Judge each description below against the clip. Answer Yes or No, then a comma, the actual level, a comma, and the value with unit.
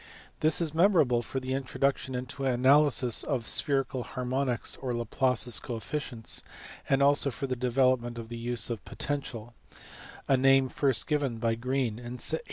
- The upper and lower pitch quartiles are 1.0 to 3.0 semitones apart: Yes, narrow, 2.4 semitones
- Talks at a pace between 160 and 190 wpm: Yes, average, 165 wpm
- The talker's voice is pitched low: Yes, low, 130 Hz